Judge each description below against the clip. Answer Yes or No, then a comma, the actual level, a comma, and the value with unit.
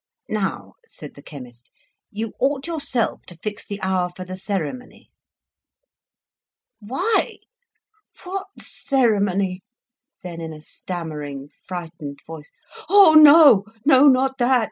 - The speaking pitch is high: Yes, high, 200 Hz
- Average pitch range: No, wide, 7.9 semitones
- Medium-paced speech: No, slow, 110 wpm